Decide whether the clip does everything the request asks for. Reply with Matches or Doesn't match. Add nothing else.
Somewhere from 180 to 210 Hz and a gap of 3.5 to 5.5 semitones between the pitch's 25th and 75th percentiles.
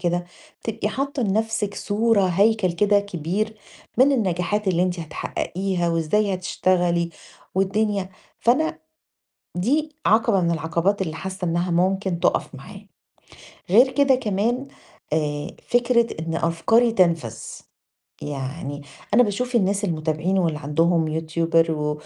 Matches